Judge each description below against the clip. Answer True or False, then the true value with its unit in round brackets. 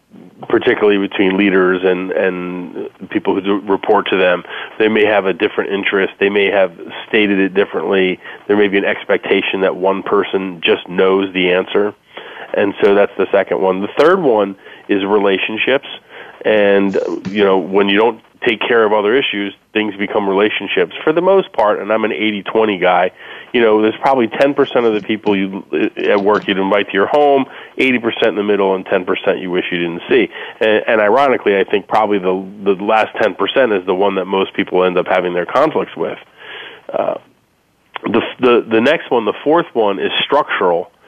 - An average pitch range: False (2.2 semitones)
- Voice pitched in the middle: False (100 Hz)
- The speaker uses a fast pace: False (190 wpm)